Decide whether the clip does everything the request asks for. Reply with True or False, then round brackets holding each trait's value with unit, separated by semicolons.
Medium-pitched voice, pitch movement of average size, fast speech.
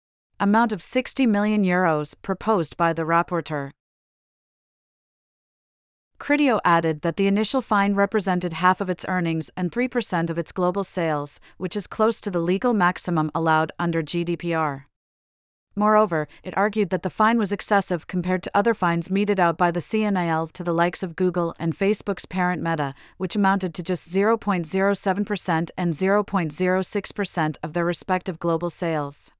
False (180 Hz; 3.4 semitones; 150 wpm)